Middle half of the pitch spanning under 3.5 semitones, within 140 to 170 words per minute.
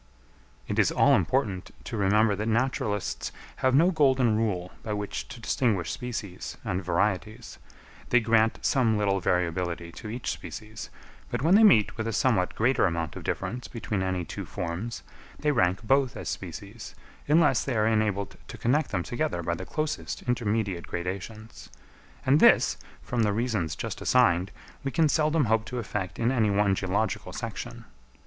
No: average, 4.7 semitones; average, 165 wpm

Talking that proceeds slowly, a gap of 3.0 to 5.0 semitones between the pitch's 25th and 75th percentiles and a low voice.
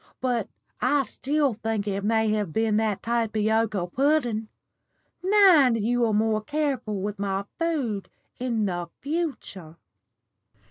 No: slow, 125 wpm; average, 4.3 semitones; high, 225 Hz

